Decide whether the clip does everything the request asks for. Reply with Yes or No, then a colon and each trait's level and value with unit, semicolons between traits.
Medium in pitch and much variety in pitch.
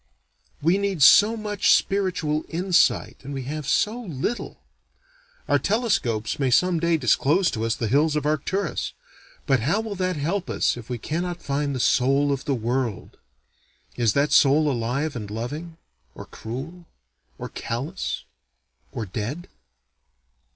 Yes: medium, 150 Hz; wide, 5.9 semitones